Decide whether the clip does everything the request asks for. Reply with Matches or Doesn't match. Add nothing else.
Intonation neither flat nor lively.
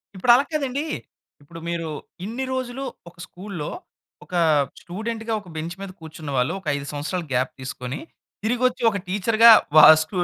Doesn't match